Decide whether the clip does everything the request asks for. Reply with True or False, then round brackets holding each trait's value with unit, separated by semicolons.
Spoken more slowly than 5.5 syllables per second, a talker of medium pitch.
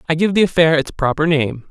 False (6.0 syllables/s; 155 Hz)